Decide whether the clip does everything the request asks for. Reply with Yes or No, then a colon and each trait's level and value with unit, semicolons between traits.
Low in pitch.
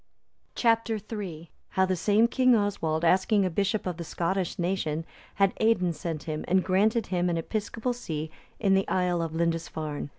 No: medium, 185 Hz